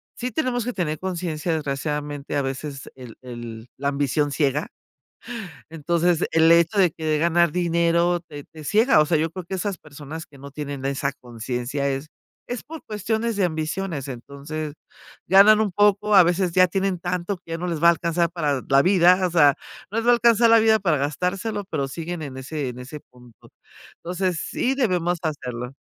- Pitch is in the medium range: Yes, medium, 165 Hz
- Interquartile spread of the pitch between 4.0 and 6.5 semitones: Yes, average, 4.6 semitones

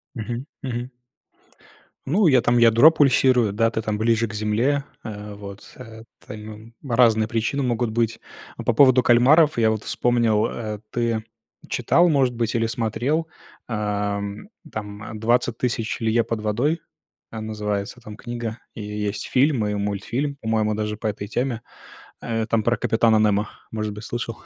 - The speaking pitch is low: Yes, low, 115 Hz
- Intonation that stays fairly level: Yes, narrow, 2.2 semitones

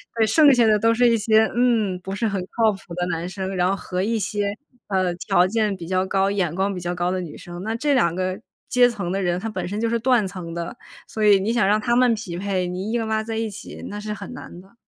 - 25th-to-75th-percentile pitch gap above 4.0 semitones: No, average, 3.5 semitones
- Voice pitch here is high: Yes, high, 200 Hz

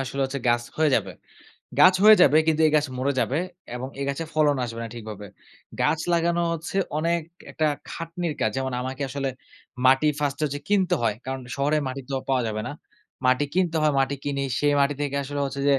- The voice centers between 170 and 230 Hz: No, medium, 140 Hz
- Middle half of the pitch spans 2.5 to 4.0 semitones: Yes, average, 3.1 semitones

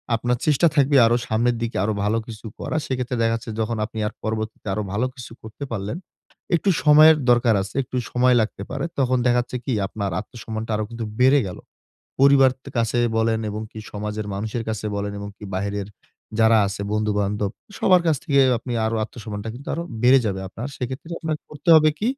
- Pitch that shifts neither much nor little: Yes, average, 3.4 semitones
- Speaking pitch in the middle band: No, low, 115 Hz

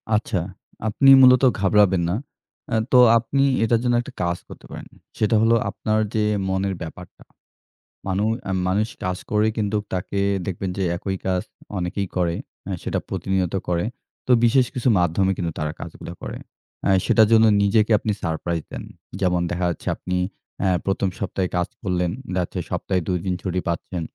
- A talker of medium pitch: No, very low, 95 Hz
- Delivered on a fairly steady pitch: No, average, 3.3 semitones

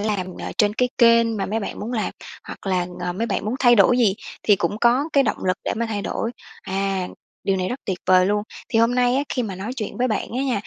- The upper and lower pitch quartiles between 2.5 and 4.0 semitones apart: Yes, average, 3.7 semitones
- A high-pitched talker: Yes, high, 215 Hz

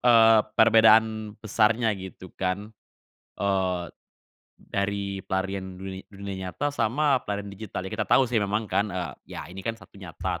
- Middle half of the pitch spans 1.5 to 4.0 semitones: Yes, average, 2.8 semitones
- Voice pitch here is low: Yes, low, 100 Hz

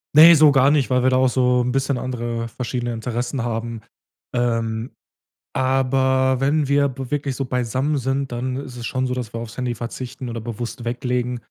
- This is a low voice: Yes, low, 125 Hz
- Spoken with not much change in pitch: Yes, narrow, 1.9 semitones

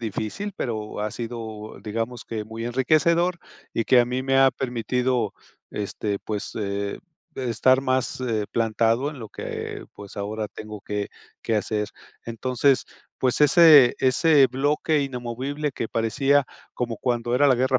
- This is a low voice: Yes, low, 120 Hz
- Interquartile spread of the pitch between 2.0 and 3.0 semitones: No, average, 3.4 semitones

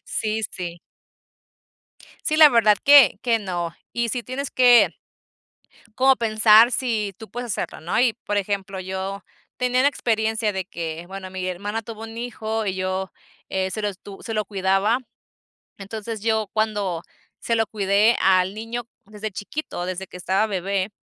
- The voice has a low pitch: No, high, 210 Hz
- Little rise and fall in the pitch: No, average, 3.2 semitones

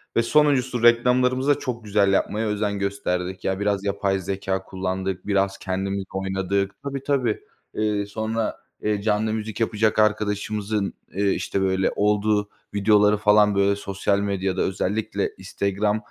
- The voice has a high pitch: No, low, 105 Hz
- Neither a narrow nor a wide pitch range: No, narrow, 1.9 semitones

